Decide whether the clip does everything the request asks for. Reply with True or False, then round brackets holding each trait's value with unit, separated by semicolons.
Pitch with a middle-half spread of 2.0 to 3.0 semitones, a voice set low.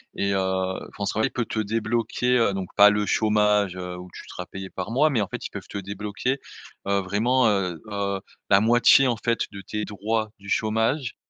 True (2.7 semitones; 105 Hz)